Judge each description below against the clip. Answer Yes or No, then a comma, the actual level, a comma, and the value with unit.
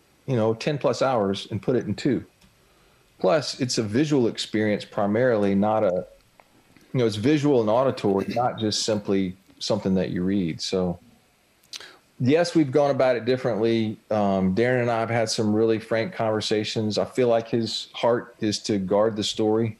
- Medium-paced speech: Yes, average, 175 wpm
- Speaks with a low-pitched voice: Yes, low, 110 Hz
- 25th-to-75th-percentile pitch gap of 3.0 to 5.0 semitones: No, narrow, 2.5 semitones